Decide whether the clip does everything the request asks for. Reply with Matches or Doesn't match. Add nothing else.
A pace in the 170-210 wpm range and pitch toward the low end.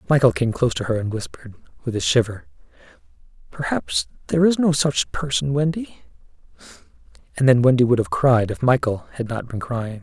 Matches